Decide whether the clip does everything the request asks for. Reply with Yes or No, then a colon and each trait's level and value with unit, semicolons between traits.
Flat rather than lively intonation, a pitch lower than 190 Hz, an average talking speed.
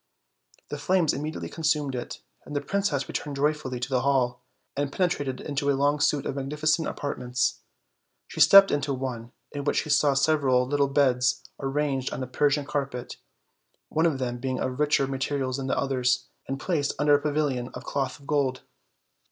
Yes: narrow, 2.1 semitones; medium, 140 Hz; average, 185 wpm